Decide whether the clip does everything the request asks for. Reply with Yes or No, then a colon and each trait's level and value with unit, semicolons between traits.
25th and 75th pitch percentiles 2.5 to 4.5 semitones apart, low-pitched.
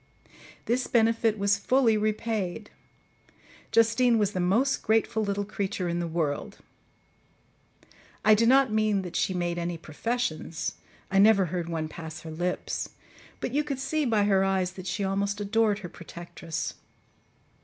No: average, 4.2 semitones; high, 200 Hz